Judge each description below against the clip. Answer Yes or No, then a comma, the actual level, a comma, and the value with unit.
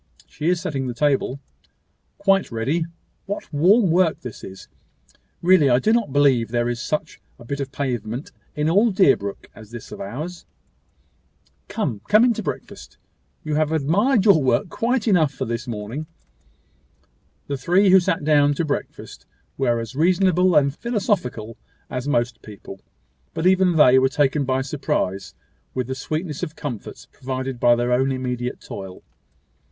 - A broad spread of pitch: Yes, wide, 6.2 semitones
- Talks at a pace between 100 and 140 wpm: No, average, 160 wpm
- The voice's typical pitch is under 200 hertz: Yes, medium, 140 Hz